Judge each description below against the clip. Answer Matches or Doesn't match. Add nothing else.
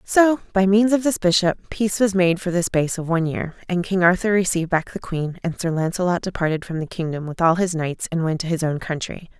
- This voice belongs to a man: Doesn't match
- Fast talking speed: Matches